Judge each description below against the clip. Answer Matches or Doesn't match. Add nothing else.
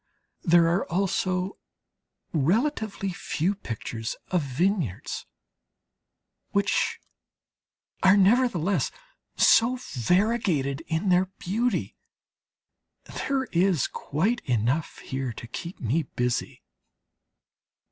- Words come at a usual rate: Doesn't match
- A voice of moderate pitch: Matches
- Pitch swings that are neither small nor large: Doesn't match